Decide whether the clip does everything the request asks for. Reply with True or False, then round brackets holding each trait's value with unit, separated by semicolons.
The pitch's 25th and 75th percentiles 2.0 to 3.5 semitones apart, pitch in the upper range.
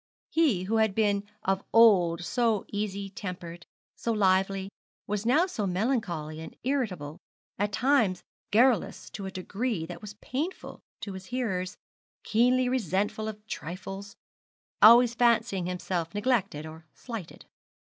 False (4.1 semitones; 205 Hz)